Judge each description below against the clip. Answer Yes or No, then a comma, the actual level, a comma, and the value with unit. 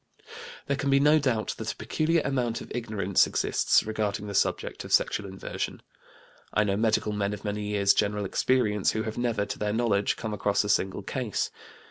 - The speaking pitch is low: Yes, low, 105 Hz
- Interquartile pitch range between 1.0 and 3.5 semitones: Yes, average, 2.8 semitones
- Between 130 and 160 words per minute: No, average, 190 wpm